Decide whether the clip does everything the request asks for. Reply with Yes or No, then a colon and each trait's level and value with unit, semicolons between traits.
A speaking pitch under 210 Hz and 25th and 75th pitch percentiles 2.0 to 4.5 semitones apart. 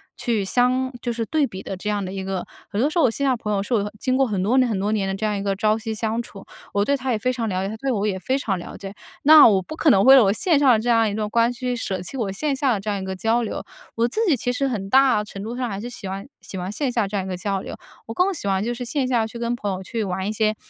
No: high, 220 Hz; average, 4.1 semitones